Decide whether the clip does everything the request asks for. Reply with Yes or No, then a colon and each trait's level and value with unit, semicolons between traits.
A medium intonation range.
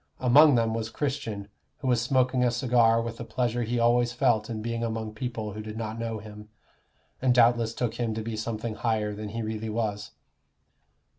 No: narrow, 1.9 semitones